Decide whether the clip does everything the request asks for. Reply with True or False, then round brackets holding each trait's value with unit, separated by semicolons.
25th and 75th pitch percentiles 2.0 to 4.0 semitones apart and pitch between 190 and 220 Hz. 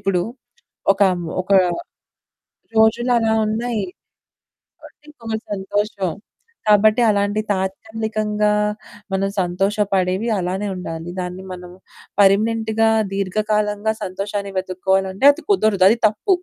True (2.4 semitones; 205 Hz)